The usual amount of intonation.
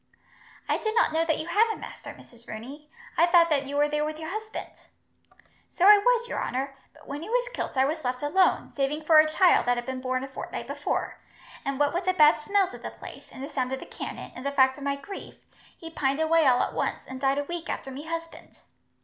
Yes: average, 4.1 semitones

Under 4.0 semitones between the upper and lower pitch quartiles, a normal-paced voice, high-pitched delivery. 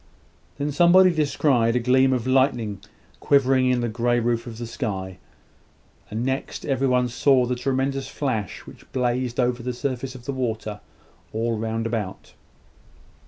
No: narrow, 2.4 semitones; average, 155 wpm; low, 125 Hz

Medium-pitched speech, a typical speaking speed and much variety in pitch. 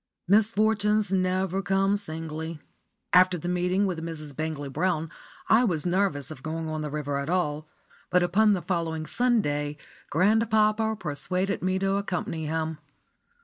No: medium, 180 Hz; average, 145 wpm; average, 4.0 semitones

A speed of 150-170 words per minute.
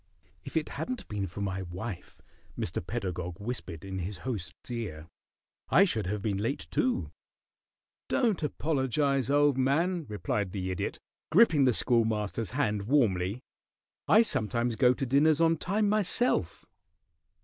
No: average, 140 wpm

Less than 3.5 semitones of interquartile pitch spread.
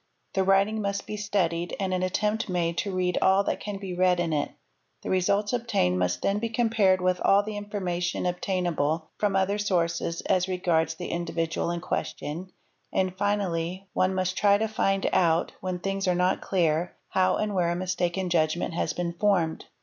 Yes: narrow, 2.4 semitones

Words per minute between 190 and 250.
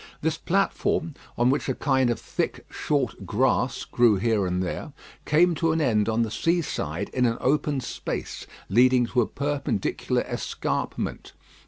No: average, 160 wpm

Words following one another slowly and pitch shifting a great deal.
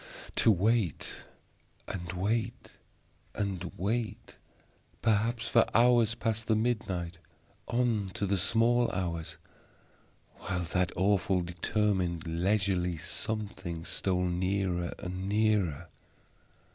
No: slow, 95 wpm; average, 3.7 semitones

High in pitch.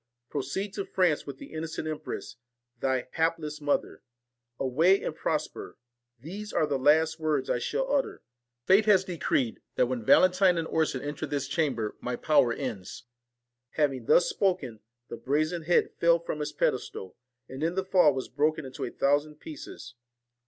No: medium, 155 Hz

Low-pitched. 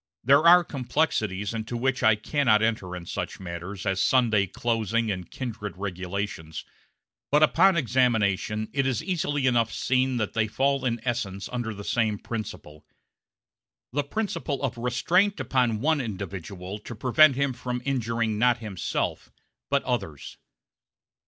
Yes: low, 115 Hz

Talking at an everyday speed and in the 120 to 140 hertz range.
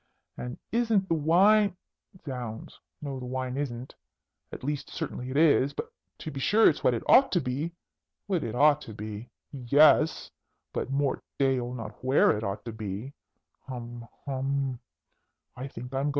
Yes: average, 150 wpm; low, 135 Hz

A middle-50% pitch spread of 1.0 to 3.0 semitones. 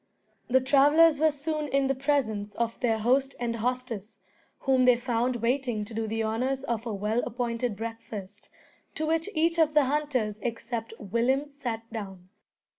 No: average, 3.6 semitones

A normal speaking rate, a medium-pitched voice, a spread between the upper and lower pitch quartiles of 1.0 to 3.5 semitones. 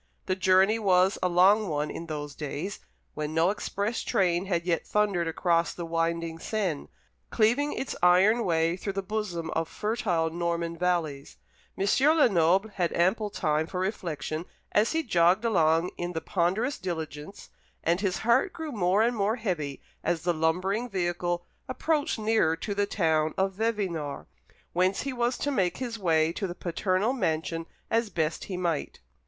No: average, 165 wpm; medium, 180 Hz; average, 4.1 semitones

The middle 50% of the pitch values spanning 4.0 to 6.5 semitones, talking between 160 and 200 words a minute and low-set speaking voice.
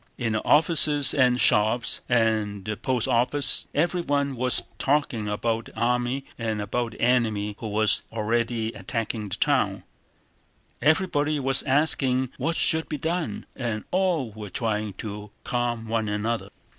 No: average, 4.3 semitones; average, 145 wpm; low, 120 Hz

